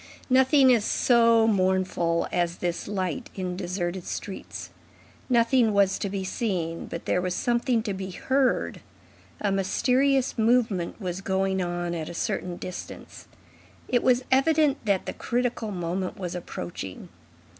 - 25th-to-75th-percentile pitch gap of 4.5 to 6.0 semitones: Yes, average, 5.1 semitones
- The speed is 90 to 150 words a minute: Yes, average, 140 wpm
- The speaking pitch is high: Yes, high, 195 Hz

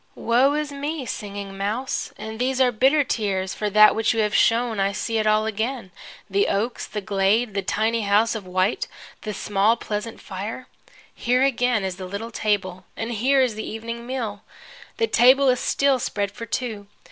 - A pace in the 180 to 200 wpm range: Yes, average, 185 wpm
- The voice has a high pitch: Yes, high, 220 Hz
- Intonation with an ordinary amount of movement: Yes, average, 3.5 semitones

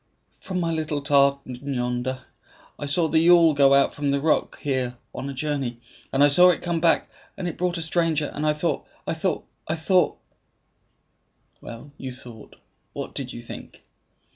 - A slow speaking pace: No, average, 185 wpm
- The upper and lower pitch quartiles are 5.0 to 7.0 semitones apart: No, average, 3.3 semitones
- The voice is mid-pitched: Yes, medium, 145 Hz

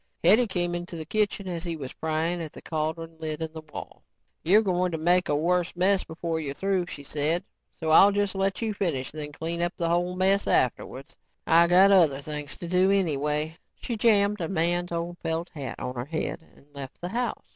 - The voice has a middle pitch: Yes, medium, 170 Hz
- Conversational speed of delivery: No, fast, 215 wpm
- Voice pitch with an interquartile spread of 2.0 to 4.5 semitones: Yes, average, 2.9 semitones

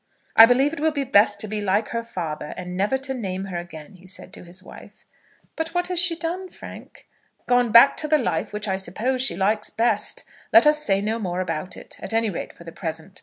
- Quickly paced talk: Yes, fast, 235 wpm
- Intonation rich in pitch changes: Yes, wide, 6.3 semitones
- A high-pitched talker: Yes, high, 215 Hz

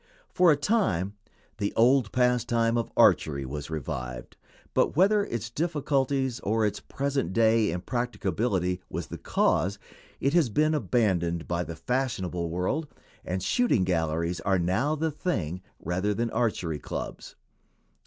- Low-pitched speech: Yes, low, 110 Hz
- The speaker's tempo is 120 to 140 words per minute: Yes, slow, 135 wpm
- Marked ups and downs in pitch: Yes, wide, 7.3 semitones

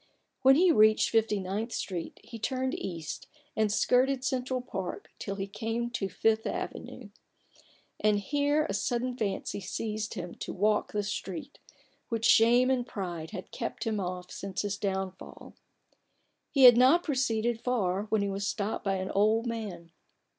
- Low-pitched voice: No, high, 215 Hz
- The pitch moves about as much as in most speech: Yes, average, 3.9 semitones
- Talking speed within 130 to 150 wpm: No, average, 160 wpm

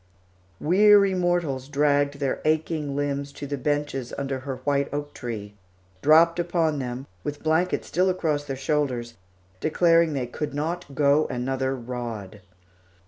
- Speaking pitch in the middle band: Yes, medium, 145 Hz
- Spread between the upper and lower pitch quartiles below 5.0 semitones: Yes, average, 3.0 semitones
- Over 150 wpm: No, average, 140 wpm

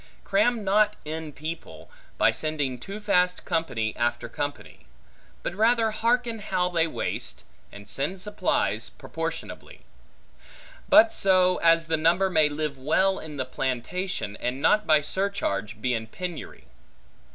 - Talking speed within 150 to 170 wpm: No, slow, 135 wpm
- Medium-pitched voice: Yes, medium, 165 Hz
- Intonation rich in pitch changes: Yes, wide, 6.2 semitones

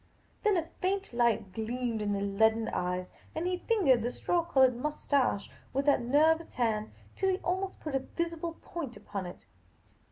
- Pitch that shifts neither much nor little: No, wide, 7.3 semitones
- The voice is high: Yes, very high, 265 Hz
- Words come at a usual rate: Yes, average, 170 wpm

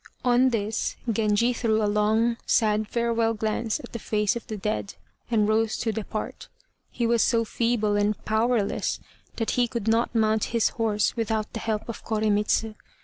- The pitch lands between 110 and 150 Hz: No, high, 220 Hz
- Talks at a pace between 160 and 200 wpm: Yes, average, 170 wpm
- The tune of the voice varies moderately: No, narrow, 1.6 semitones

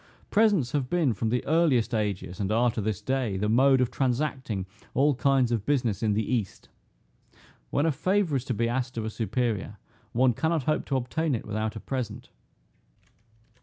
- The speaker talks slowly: No, average, 185 wpm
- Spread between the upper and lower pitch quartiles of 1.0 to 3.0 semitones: No, average, 4.1 semitones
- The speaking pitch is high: No, low, 125 Hz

